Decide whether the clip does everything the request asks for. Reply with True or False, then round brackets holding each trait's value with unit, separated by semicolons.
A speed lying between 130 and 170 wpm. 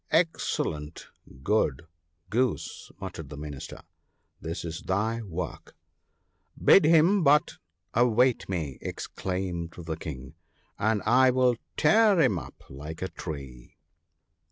True (140 wpm)